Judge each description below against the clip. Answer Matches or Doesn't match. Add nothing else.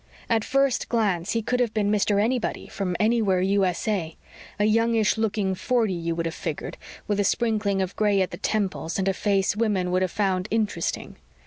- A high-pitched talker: Matches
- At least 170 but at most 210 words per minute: Matches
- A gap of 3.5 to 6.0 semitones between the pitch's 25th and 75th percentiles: Doesn't match